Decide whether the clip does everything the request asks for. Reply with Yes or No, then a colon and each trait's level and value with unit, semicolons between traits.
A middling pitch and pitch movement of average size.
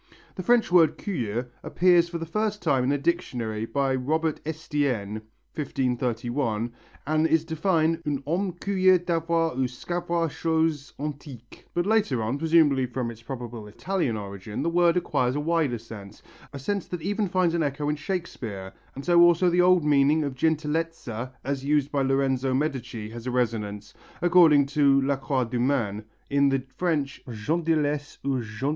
Yes: medium, 145 Hz; average, 5.0 semitones